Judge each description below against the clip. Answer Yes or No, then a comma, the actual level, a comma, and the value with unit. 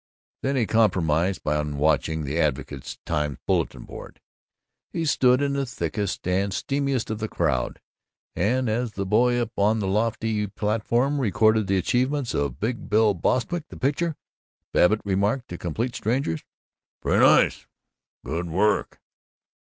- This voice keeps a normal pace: Yes, average, 145 wpm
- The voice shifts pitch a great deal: Yes, wide, 6.2 semitones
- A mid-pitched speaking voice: No, low, 105 Hz